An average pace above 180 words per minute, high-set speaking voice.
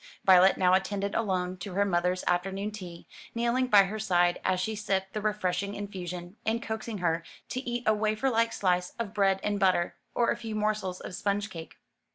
Yes: average, 190 wpm; high, 200 Hz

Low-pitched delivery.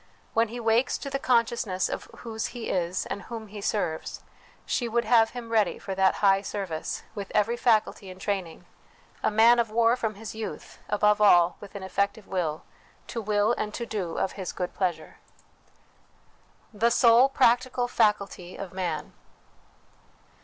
No: high, 210 Hz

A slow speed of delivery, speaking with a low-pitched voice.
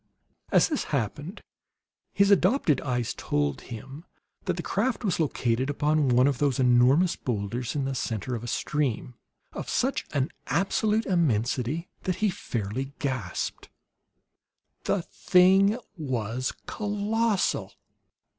No: slow, 120 wpm; medium, 145 Hz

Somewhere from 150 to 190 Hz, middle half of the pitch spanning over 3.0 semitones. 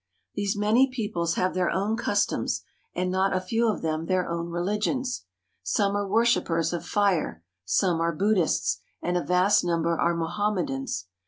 Yes: medium, 185 Hz; average, 3.6 semitones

